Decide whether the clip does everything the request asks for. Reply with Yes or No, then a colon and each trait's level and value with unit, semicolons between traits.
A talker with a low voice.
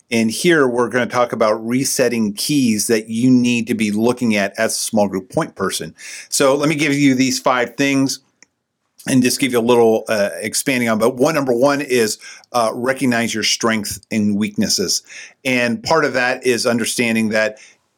Yes: low, 120 Hz